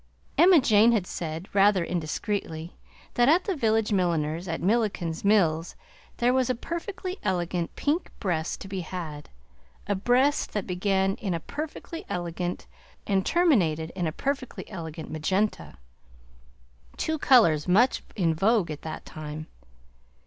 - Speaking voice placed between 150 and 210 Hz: Yes, high, 190 Hz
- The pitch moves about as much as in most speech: No, wide, 6.3 semitones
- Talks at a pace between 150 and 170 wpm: No, average, 140 wpm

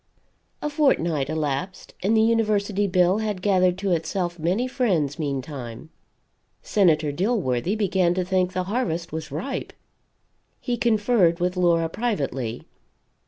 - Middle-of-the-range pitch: Yes, medium, 180 Hz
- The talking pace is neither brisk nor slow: No, slow, 125 wpm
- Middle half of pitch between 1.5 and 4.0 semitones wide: No, average, 4.7 semitones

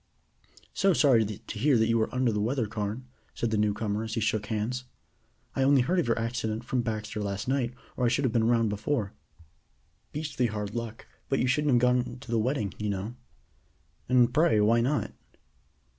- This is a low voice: Yes, low, 115 Hz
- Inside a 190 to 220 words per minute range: Yes, average, 200 wpm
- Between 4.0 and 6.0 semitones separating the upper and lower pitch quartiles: No, average, 2.8 semitones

